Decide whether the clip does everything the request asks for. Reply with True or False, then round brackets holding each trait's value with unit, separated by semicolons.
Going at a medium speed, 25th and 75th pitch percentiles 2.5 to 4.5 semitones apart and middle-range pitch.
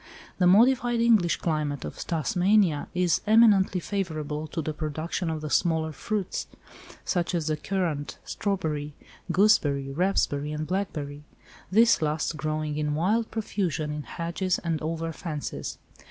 False (130 wpm; 4.0 semitones; 165 Hz)